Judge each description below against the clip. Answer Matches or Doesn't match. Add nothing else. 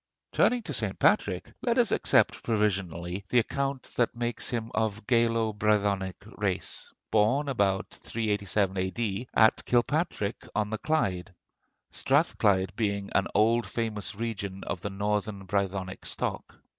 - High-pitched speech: Doesn't match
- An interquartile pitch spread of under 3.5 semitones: Matches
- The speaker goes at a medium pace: Doesn't match